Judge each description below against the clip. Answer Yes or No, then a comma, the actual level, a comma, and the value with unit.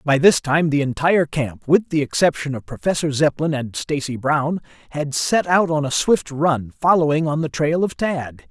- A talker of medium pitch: Yes, medium, 150 Hz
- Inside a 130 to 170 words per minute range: No, average, 200 wpm